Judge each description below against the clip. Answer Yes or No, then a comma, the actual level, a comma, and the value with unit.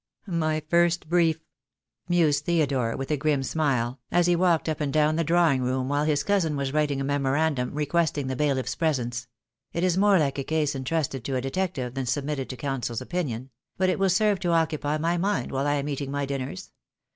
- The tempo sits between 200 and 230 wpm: Yes, fast, 205 wpm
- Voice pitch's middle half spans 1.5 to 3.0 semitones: No, average, 3.7 semitones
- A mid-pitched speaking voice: Yes, medium, 150 Hz